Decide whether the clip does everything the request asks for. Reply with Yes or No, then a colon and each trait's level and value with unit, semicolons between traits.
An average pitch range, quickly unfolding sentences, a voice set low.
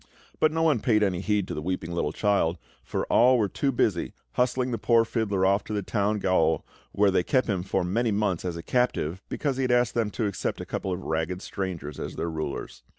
Yes: average, 4.7 semitones; fast, 230 wpm; low, 100 Hz